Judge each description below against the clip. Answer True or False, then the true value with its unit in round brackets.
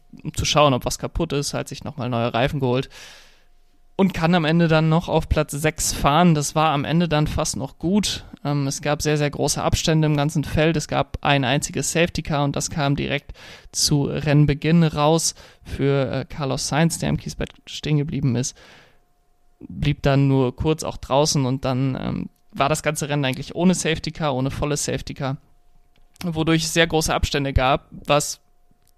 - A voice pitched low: False (145 Hz)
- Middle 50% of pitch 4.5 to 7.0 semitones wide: False (2.7 semitones)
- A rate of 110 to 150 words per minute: False (190 wpm)